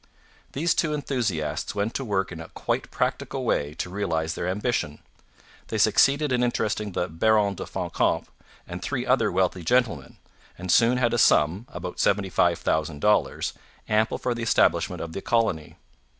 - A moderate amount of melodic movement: No, wide, 5.7 semitones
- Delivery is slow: No, average, 155 wpm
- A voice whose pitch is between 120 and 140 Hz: No, low, 100 Hz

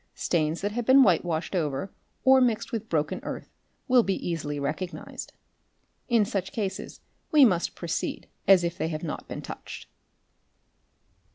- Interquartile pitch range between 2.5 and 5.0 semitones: No, wide, 5.6 semitones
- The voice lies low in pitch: No, medium, 185 Hz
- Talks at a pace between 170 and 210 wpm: No, average, 155 wpm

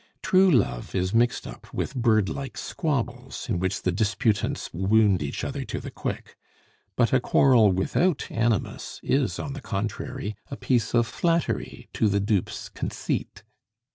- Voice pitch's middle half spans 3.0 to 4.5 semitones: No, average, 5.0 semitones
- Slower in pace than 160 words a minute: Yes, average, 150 wpm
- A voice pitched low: Yes, low, 115 Hz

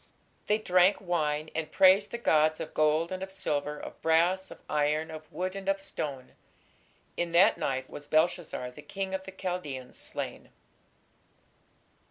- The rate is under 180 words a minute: Yes, average, 160 wpm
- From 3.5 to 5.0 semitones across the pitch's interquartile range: Yes, average, 3.9 semitones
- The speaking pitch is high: No, medium, 165 Hz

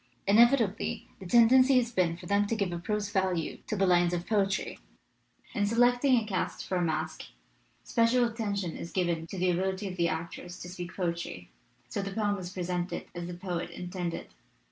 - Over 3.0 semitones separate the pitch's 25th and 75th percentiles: Yes, average, 3.4 semitones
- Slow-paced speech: No, average, 190 wpm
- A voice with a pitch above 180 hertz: Yes, high, 190 Hz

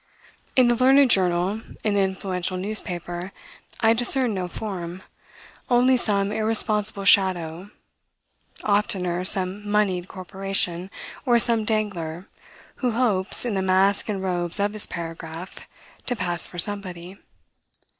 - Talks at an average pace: No, slow, 125 wpm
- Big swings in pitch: No, average, 3.0 semitones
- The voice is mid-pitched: No, high, 195 Hz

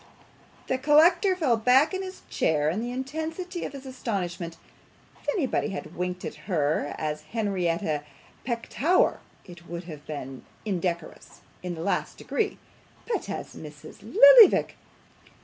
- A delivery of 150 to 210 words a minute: No, slow, 135 wpm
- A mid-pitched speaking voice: No, high, 210 Hz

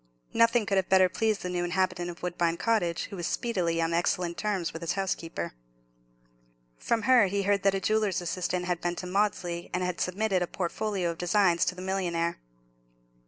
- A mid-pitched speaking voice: Yes, medium, 180 Hz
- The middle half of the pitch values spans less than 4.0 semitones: Yes, narrow, 2.5 semitones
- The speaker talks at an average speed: Yes, average, 190 wpm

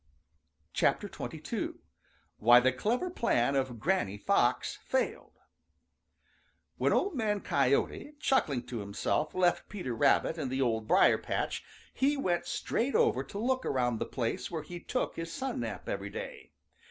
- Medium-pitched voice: Yes, medium, 165 Hz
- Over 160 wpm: No, average, 145 wpm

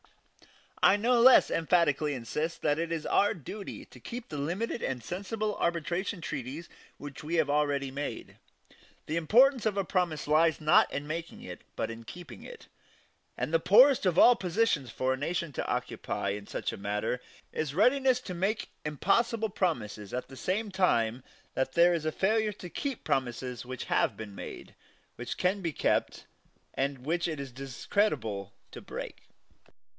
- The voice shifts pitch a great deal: Yes, wide, 6.7 semitones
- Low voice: No, medium, 165 Hz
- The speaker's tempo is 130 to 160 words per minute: No, average, 170 wpm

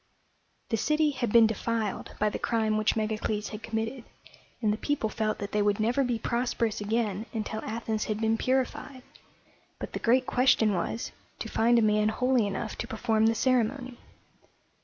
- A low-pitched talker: No, high, 225 Hz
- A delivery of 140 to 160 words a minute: No, average, 175 wpm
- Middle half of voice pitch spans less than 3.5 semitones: Yes, narrow, 2.4 semitones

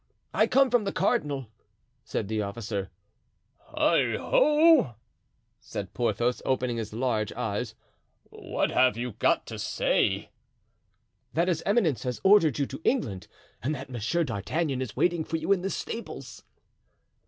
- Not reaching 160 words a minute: Yes, average, 140 wpm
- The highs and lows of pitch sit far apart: Yes, wide, 7.6 semitones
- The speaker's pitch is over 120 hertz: Yes, low, 135 Hz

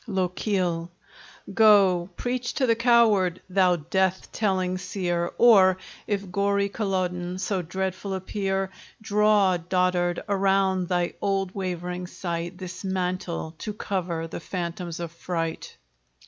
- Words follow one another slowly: Yes, slow, 120 wpm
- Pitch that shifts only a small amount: Yes, narrow, 2.0 semitones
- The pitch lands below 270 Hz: Yes, medium, 185 Hz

